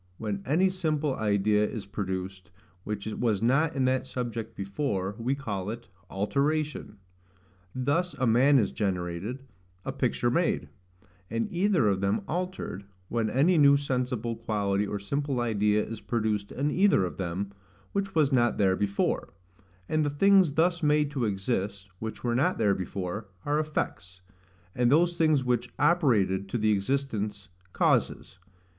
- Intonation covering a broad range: Yes, wide, 6.2 semitones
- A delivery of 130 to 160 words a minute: Yes, average, 150 wpm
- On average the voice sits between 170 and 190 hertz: No, low, 115 Hz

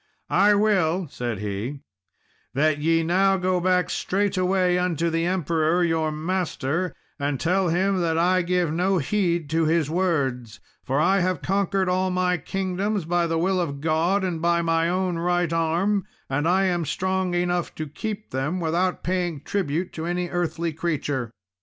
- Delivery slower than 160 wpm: No, average, 165 wpm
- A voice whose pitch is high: No, medium, 175 Hz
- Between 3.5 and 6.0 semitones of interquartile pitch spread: No, narrow, 2.5 semitones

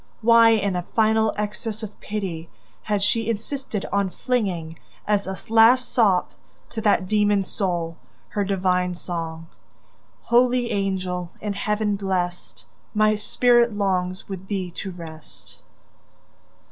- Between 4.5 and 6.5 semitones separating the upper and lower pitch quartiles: No, average, 3.2 semitones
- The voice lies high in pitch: Yes, high, 200 Hz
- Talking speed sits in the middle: No, slow, 125 wpm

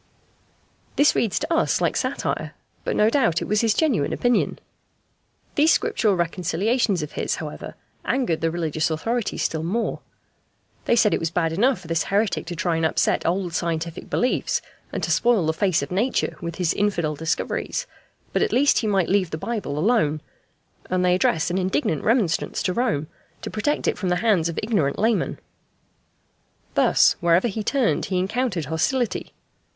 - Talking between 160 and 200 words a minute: Yes, average, 175 wpm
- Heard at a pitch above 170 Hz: Yes, medium, 185 Hz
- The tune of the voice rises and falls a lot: Yes, wide, 5.7 semitones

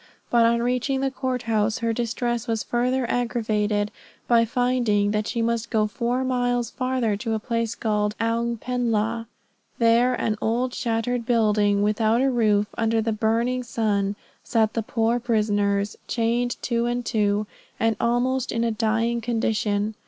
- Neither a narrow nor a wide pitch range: No, narrow, 2.0 semitones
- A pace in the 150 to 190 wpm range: Yes, average, 160 wpm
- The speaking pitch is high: Yes, high, 230 Hz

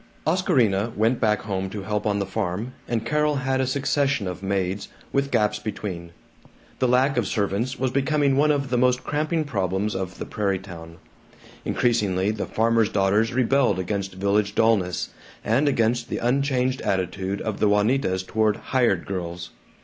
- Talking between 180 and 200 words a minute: No, average, 165 wpm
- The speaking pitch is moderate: No, low, 110 Hz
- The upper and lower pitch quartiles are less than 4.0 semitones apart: No, average, 4.9 semitones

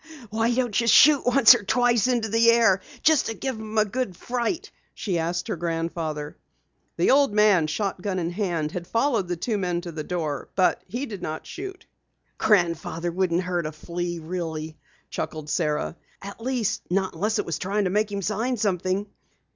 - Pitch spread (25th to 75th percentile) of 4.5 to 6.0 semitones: Yes, average, 4.9 semitones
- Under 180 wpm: No, average, 185 wpm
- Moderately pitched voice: No, high, 195 Hz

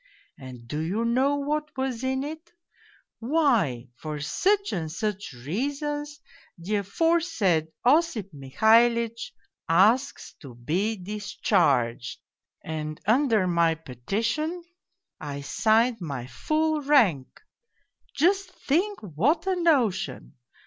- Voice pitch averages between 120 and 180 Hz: No, high, 220 Hz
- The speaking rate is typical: No, slow, 105 wpm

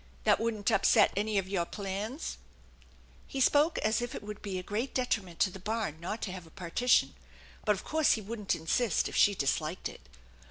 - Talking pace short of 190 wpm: No, fast, 205 wpm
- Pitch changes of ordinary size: Yes, average, 3.7 semitones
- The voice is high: Yes, high, 205 Hz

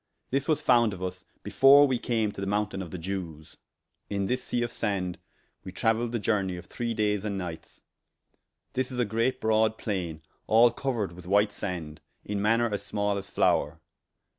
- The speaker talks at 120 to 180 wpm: No, average, 190 wpm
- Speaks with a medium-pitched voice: No, low, 105 Hz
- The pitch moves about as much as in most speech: Yes, average, 3.7 semitones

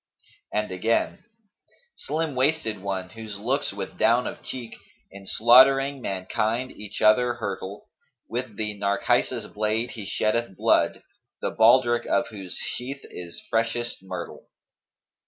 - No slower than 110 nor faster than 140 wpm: Yes, slow, 135 wpm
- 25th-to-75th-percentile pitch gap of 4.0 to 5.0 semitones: No, average, 3.4 semitones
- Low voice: Yes, low, 115 Hz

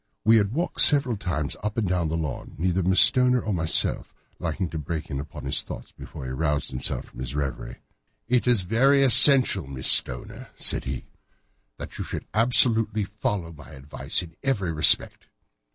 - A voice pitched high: No, very low, 90 Hz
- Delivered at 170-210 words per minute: Yes, average, 180 wpm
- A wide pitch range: Yes, wide, 6.9 semitones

